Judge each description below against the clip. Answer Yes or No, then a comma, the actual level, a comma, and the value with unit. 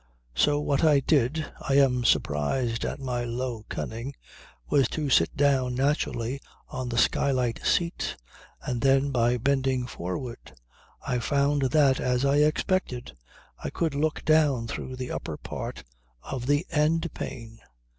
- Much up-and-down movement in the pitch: No, average, 2.9 semitones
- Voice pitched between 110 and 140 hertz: Yes, low, 135 Hz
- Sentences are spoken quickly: No, average, 145 wpm